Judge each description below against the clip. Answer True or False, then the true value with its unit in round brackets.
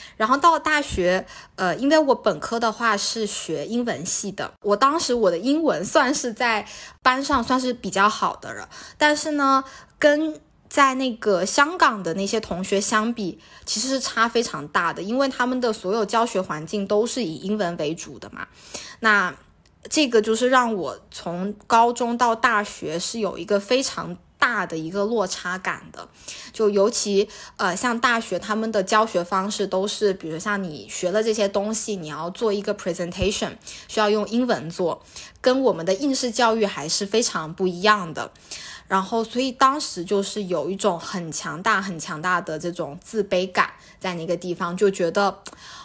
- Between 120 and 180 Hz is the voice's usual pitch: False (210 Hz)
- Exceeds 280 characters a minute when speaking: False (270 characters per minute)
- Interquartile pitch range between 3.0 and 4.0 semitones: False (4.6 semitones)